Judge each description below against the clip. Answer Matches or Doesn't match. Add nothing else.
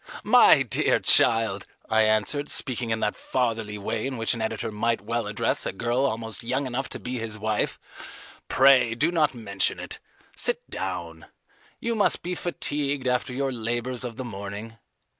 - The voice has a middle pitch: Doesn't match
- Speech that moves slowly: Doesn't match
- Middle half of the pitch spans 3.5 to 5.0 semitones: Doesn't match